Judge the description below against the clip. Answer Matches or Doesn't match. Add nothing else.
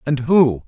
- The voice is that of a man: Matches